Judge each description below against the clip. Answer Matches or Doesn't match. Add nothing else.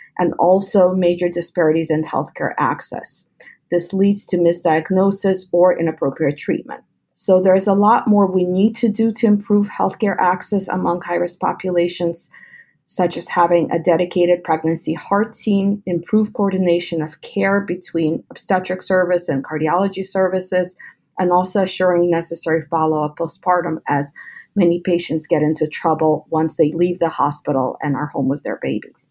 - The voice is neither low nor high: Matches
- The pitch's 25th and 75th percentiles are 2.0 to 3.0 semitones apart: Matches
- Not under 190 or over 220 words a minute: Doesn't match